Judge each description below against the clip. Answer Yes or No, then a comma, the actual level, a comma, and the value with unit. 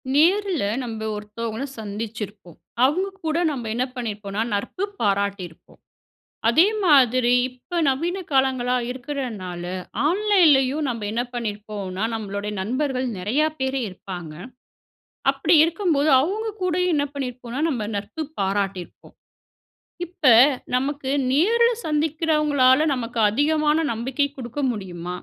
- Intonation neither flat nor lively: No, wide, 6.3 semitones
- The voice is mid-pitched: No, very high, 255 Hz